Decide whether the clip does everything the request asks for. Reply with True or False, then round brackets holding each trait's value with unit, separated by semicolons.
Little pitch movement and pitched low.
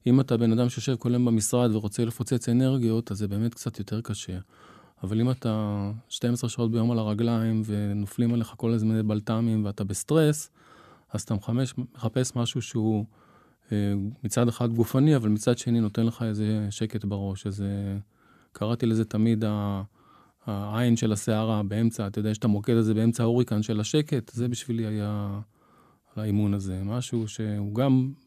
True (2.3 semitones; 110 Hz)